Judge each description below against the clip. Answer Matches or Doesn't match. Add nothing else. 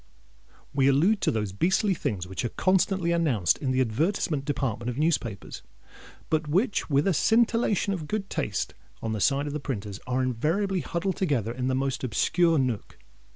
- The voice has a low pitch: Doesn't match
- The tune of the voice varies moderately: Doesn't match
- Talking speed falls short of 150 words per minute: Doesn't match